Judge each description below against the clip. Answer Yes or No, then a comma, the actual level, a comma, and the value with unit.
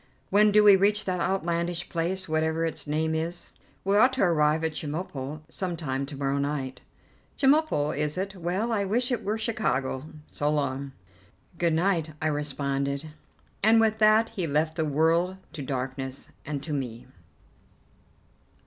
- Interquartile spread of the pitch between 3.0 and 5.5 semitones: Yes, average, 5.0 semitones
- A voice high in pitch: No, medium, 160 Hz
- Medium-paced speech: Yes, average, 160 wpm